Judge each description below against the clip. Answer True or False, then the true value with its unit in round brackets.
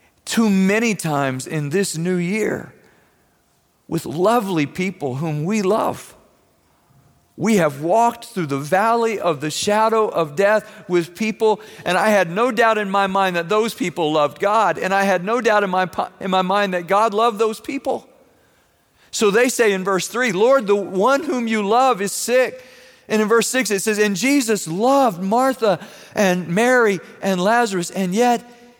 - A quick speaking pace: False (175 wpm)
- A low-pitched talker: False (210 Hz)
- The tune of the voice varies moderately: True (3.9 semitones)